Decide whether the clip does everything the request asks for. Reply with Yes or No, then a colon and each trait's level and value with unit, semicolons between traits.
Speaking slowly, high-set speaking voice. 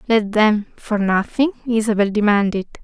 Yes: slow, 125 wpm; high, 215 Hz